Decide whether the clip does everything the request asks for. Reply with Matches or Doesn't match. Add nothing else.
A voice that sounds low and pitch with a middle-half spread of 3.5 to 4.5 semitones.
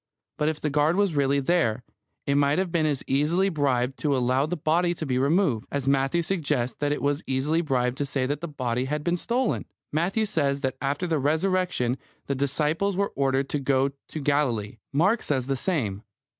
Doesn't match